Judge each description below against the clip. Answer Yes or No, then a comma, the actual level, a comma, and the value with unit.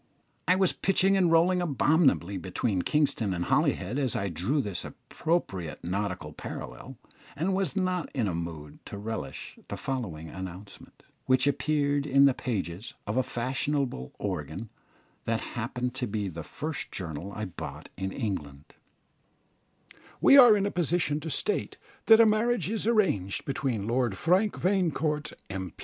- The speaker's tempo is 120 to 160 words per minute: Yes, average, 150 wpm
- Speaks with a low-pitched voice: Yes, low, 125 Hz